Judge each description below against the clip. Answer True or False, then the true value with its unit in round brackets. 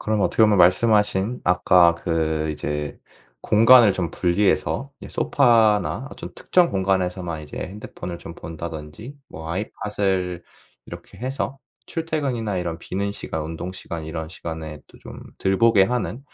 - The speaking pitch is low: True (95 Hz)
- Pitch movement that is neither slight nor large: True (4.6 semitones)